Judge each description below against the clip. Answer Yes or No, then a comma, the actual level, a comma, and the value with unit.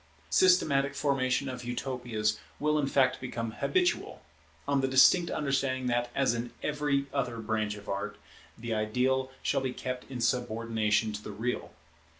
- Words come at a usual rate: Yes, average, 155 wpm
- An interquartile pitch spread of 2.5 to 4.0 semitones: Yes, average, 3.2 semitones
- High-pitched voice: No, low, 125 Hz